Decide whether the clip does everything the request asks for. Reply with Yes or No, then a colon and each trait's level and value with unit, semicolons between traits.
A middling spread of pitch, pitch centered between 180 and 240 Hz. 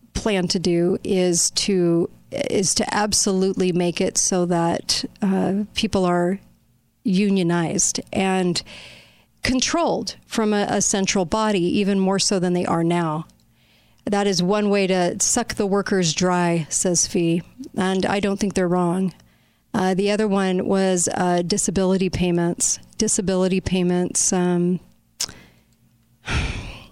No: narrow, 2.2 semitones; medium, 185 Hz